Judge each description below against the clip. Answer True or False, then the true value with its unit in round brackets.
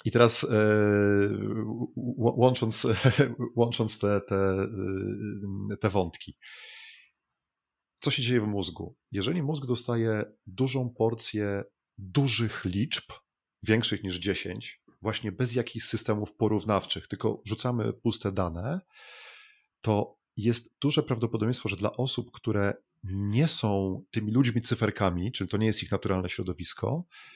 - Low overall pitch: True (110 Hz)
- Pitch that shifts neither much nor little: True (3.6 semitones)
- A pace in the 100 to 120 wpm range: True (115 wpm)